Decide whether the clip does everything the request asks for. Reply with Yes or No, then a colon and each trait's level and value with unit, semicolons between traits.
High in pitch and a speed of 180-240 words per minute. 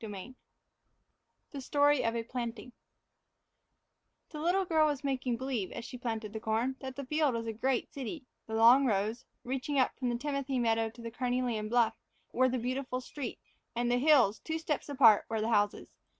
Yes: very high, 250 Hz; average, 185 wpm